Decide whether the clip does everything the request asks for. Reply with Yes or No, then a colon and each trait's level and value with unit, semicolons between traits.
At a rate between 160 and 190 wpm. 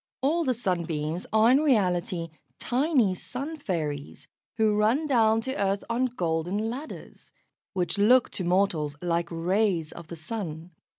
No: average, 140 wpm